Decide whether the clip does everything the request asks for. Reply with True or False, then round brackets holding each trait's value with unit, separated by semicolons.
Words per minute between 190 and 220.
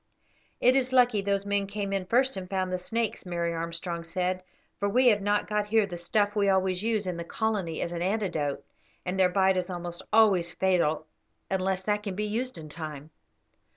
True (200 wpm)